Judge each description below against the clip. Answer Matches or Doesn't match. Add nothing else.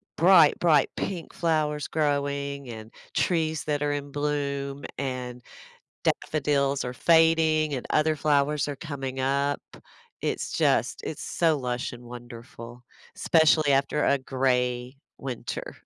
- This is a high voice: Doesn't match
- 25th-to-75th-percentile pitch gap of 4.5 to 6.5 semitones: Doesn't match